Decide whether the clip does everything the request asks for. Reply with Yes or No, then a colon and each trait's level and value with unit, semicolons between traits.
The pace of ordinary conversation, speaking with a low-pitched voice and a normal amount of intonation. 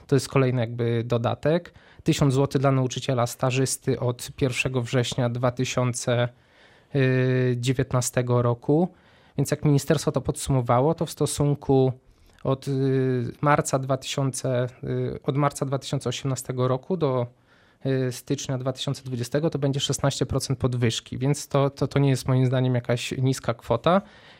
No: average, 120 wpm; low, 130 Hz; narrow, 2.1 semitones